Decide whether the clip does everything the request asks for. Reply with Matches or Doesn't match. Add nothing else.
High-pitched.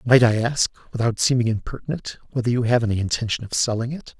Doesn't match